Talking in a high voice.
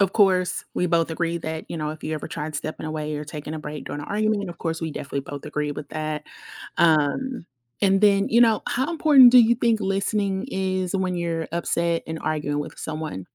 No: medium, 170 Hz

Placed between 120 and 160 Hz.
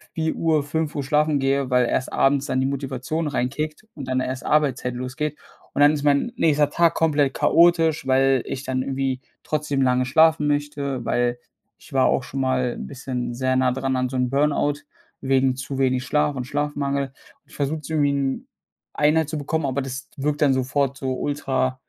Yes: medium, 140 Hz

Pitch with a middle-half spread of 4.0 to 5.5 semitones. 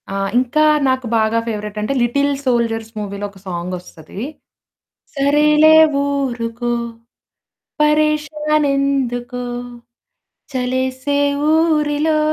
Yes: average, 4.6 semitones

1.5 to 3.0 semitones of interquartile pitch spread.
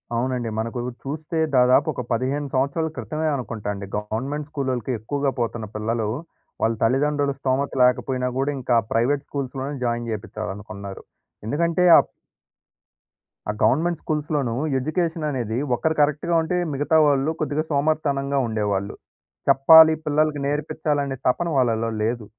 No: average, 4.2 semitones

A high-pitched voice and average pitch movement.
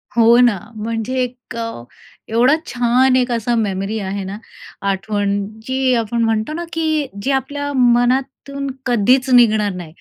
Yes: high, 240 Hz; average, 3.3 semitones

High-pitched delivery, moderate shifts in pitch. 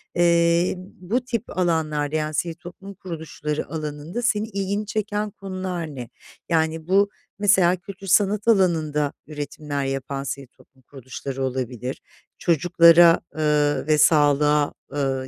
No: medium, 160 Hz; average, 4.2 semitones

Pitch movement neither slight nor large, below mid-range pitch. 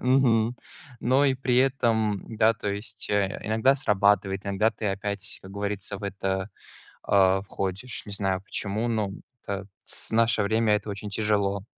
No: narrow, 2.3 semitones; low, 105 Hz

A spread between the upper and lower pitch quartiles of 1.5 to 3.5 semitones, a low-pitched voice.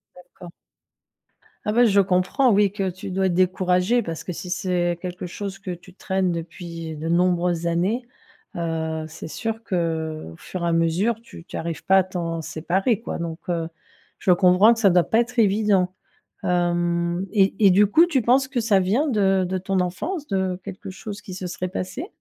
No: average, 2.9 semitones; medium, 185 Hz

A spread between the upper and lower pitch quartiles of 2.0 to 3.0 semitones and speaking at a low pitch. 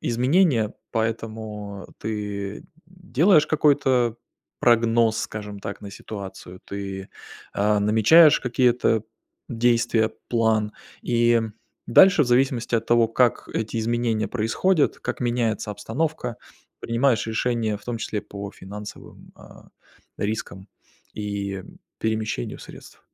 Yes: average, 2.7 semitones; low, 115 Hz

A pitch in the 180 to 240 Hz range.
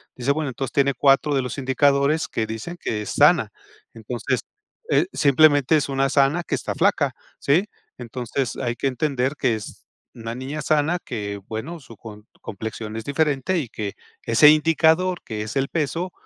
No: low, 135 Hz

